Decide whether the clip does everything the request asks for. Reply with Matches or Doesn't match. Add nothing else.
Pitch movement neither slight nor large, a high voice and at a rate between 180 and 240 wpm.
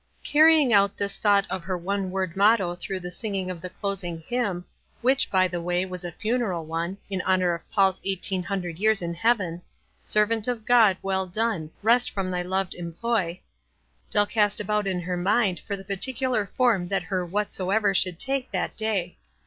Matches